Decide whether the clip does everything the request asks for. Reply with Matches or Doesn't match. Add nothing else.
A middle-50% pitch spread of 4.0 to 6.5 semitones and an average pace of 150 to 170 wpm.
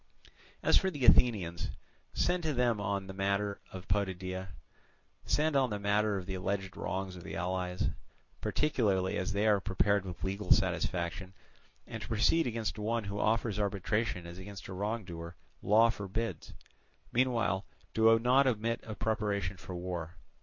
Doesn't match